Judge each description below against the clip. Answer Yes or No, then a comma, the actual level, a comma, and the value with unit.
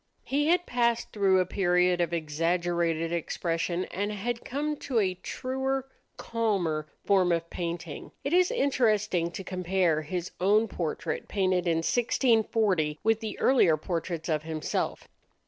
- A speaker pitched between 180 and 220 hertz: Yes, medium, 185 Hz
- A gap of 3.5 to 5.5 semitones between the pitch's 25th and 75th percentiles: Yes, average, 5.2 semitones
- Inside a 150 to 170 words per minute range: No, average, 140 wpm